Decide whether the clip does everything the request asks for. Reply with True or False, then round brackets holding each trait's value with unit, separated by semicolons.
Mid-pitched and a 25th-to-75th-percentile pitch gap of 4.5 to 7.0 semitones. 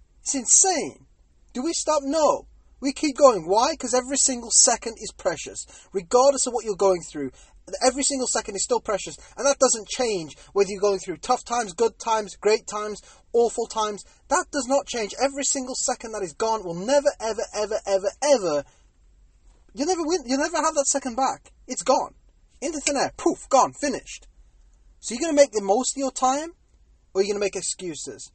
False (240 Hz; 5.5 semitones)